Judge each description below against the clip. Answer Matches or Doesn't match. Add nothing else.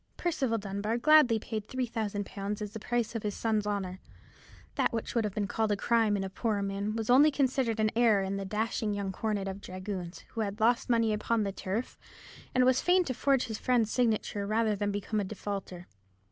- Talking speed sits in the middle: Doesn't match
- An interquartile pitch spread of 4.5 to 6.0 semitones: Doesn't match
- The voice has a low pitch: Doesn't match